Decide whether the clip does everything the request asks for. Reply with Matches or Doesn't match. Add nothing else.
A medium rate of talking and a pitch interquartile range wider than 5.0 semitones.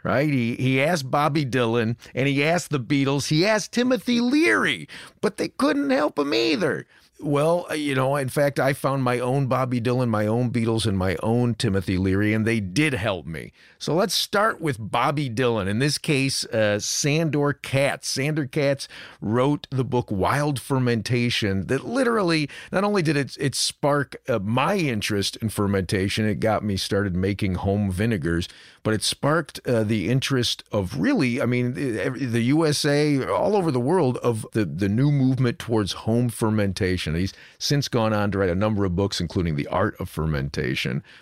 Matches